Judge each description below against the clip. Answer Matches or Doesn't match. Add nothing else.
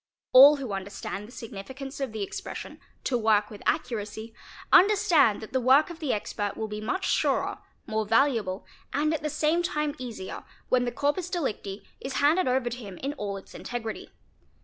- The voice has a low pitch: Doesn't match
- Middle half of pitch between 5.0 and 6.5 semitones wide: Matches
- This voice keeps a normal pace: Matches